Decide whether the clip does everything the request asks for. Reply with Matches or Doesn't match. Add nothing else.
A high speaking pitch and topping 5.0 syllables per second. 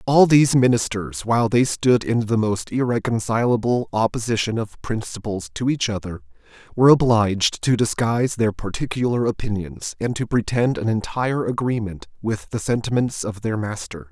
Doesn't match